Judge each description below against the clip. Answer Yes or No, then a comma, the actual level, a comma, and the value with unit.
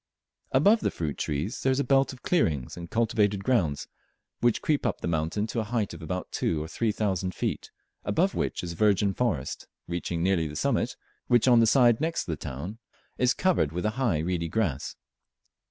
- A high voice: No, low, 105 Hz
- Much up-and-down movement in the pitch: Yes, wide, 6.5 semitones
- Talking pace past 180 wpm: Yes, average, 200 wpm